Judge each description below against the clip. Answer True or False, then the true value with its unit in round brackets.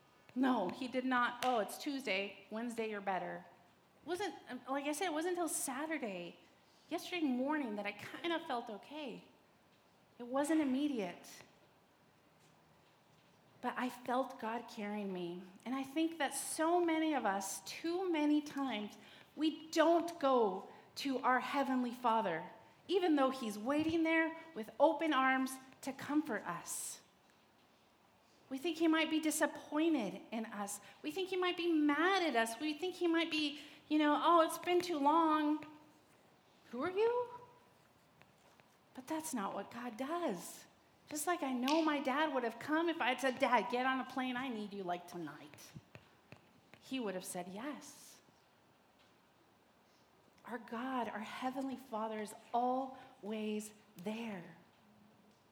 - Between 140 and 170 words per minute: True (150 wpm)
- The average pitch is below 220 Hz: False (265 Hz)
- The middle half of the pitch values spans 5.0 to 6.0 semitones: True (5.6 semitones)